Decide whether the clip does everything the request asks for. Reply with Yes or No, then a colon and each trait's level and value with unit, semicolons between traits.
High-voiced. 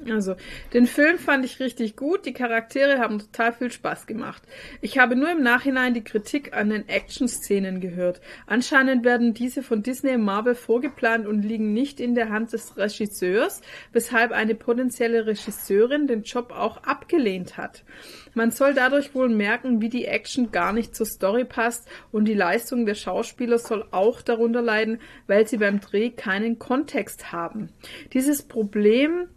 Yes: high, 235 Hz